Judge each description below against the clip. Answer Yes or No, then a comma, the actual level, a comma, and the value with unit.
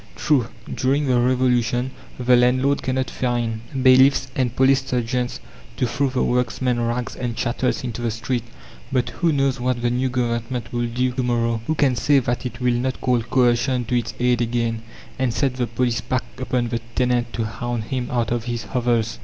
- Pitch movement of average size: No, narrow, 1.4 semitones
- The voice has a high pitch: No, low, 125 Hz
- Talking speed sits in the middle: Yes, average, 190 wpm